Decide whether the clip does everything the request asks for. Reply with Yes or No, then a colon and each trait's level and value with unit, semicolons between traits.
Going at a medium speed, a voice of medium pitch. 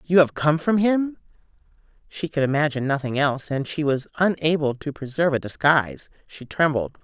Yes: average, 170 wpm; medium, 150 Hz